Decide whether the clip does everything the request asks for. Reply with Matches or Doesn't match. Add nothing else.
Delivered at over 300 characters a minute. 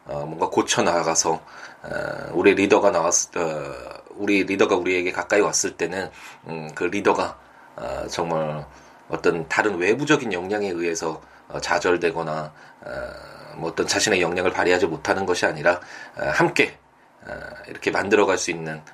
Matches